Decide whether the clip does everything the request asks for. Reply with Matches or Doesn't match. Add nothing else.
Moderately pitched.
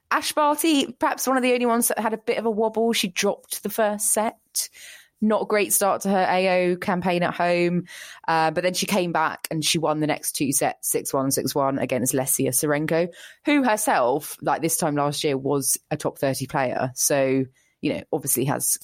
Matches